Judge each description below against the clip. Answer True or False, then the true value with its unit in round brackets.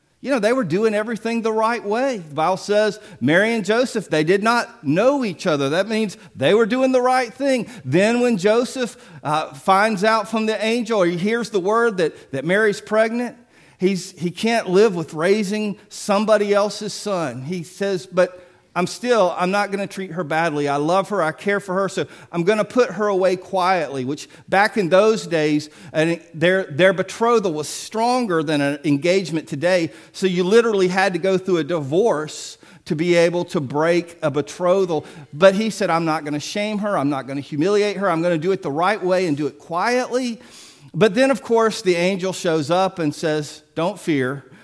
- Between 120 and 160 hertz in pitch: False (190 Hz)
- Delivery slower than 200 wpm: False (205 wpm)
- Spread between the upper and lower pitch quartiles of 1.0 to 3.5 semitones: False (4.7 semitones)